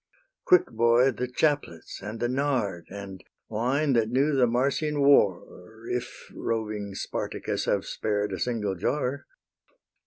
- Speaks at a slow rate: Yes, slow, 130 wpm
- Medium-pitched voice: No, low, 120 Hz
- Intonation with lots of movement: No, average, 4.6 semitones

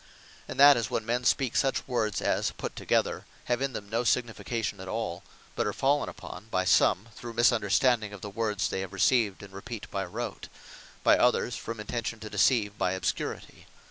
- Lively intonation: No, average, 3.1 semitones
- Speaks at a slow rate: No, average, 190 wpm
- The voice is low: Yes, low, 115 Hz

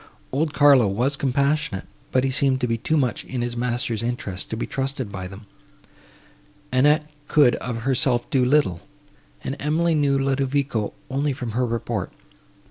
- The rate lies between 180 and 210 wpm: No, average, 160 wpm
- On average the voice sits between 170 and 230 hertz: No, low, 130 Hz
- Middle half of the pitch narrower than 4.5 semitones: Yes, average, 3.0 semitones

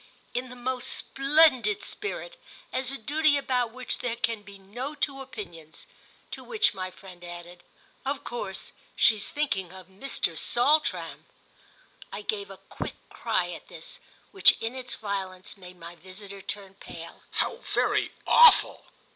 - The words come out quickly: No, average, 145 wpm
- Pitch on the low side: No, high, 230 Hz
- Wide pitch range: Yes, wide, 6.3 semitones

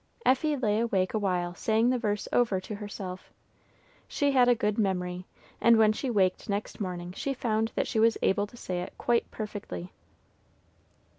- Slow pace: No, average, 170 wpm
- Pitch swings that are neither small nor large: Yes, average, 3.9 semitones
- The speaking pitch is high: Yes, high, 210 Hz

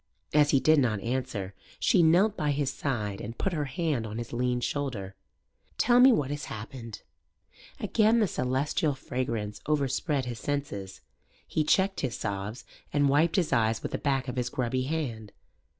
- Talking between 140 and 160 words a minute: No, average, 170 wpm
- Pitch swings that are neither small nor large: Yes, average, 4.5 semitones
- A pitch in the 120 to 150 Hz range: Yes, low, 135 Hz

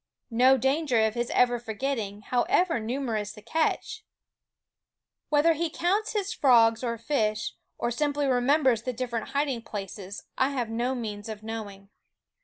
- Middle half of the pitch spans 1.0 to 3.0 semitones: No, average, 4.3 semitones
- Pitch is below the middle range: No, high, 245 Hz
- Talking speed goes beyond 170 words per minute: No, average, 155 wpm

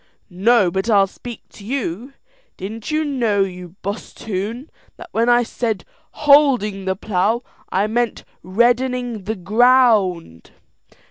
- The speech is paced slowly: Yes, slow, 125 wpm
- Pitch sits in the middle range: No, high, 220 Hz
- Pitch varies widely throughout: No, average, 4.1 semitones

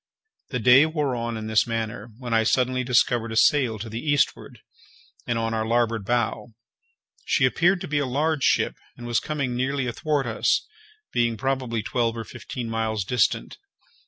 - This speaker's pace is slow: No, average, 175 wpm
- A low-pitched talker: Yes, low, 120 Hz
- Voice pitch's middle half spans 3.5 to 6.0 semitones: No, average, 2.9 semitones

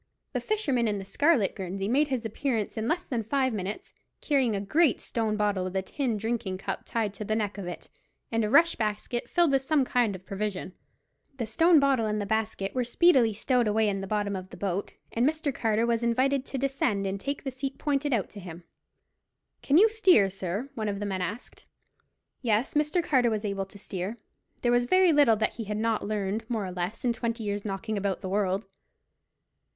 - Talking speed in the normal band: No, fast, 215 wpm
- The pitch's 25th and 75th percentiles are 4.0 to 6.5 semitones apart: Yes, average, 4.7 semitones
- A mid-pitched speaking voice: No, high, 220 Hz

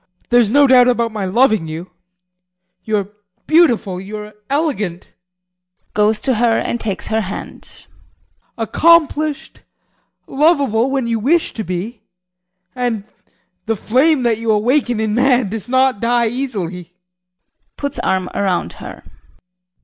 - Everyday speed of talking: No, slow, 130 wpm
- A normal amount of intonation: Yes, average, 4.0 semitones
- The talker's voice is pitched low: No, high, 230 Hz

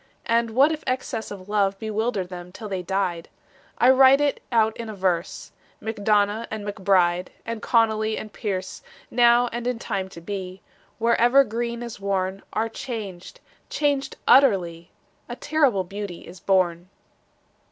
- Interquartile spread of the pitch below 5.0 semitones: Yes, average, 3.9 semitones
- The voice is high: Yes, high, 215 Hz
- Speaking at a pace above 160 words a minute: No, average, 150 wpm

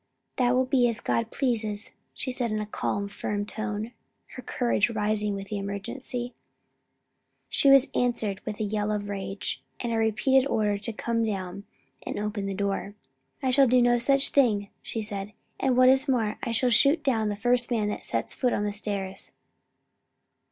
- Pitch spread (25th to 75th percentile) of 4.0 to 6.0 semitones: No, average, 3.2 semitones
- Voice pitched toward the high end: Yes, high, 220 Hz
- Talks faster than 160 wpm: Yes, average, 185 wpm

